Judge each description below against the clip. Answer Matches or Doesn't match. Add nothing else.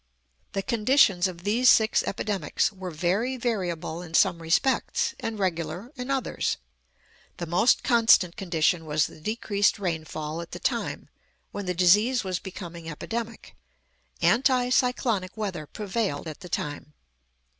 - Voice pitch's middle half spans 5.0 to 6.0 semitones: Matches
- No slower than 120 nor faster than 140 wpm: Matches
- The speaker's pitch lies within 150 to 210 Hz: Matches